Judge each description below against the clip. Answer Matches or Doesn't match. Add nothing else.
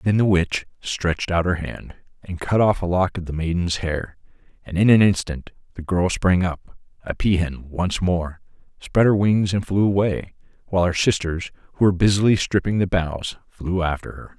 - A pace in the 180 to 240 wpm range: Matches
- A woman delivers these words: Doesn't match